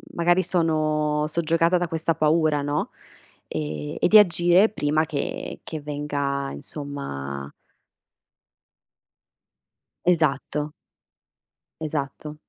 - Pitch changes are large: No, narrow, 2.6 semitones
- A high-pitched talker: No, medium, 150 Hz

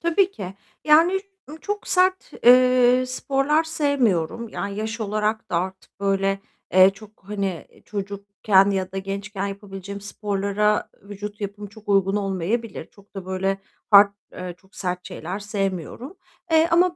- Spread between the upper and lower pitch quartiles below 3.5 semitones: No, average, 3.9 semitones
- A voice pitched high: Yes, high, 205 Hz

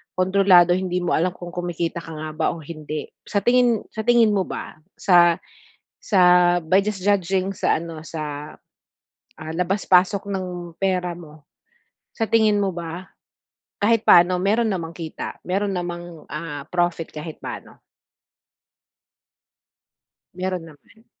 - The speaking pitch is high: No, medium, 180 Hz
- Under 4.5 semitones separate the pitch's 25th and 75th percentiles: Yes, average, 2.9 semitones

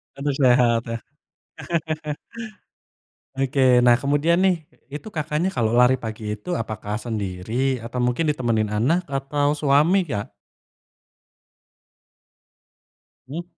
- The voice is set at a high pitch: No, low, 130 Hz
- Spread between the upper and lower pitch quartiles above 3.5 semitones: Yes, average, 4.4 semitones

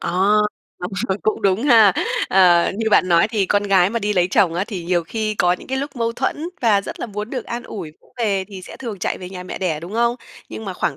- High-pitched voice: Yes, high, 200 Hz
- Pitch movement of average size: Yes, average, 3.8 semitones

